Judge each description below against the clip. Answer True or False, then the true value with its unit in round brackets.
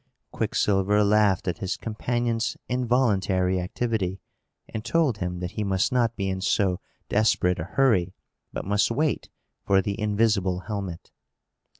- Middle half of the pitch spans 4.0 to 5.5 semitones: False (3.3 semitones)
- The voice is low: True (105 Hz)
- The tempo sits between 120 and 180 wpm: True (135 wpm)